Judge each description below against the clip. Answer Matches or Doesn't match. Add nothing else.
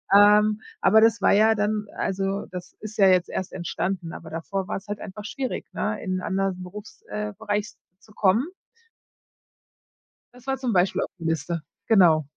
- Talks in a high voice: Matches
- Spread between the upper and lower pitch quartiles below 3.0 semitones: Matches